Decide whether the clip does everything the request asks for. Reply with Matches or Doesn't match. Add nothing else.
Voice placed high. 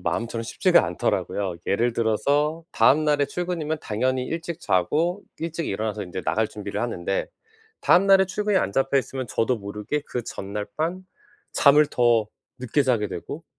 Doesn't match